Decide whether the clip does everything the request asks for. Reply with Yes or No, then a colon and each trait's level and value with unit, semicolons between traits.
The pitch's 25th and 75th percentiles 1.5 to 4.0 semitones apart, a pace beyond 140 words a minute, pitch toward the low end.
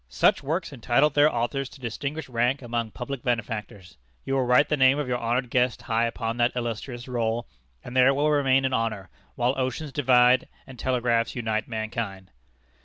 Yes: narrow, 2.5 semitones; average, 180 wpm; low, 125 Hz